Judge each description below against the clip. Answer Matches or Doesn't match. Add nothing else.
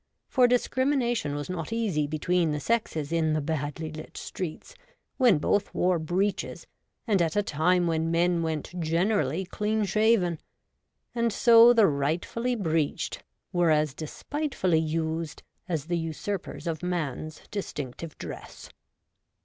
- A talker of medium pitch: Matches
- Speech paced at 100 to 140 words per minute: Matches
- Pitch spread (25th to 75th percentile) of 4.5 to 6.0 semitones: Matches